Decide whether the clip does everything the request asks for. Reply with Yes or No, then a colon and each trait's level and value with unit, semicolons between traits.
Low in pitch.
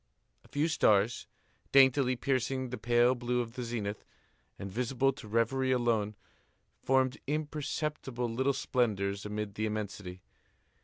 Yes: low, 120 Hz